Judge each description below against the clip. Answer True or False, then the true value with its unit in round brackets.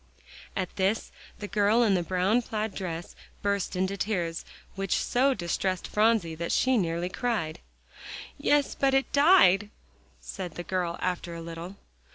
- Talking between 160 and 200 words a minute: False (150 wpm)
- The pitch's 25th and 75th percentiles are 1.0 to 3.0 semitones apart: False (4.0 semitones)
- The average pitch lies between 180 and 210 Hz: True (190 Hz)